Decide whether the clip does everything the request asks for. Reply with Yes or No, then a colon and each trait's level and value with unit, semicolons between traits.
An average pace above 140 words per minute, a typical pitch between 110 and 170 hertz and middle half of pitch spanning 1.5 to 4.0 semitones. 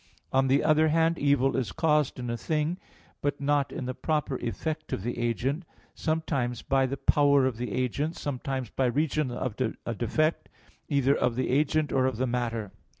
Yes: average, 185 wpm; low, 135 Hz; average, 3.4 semitones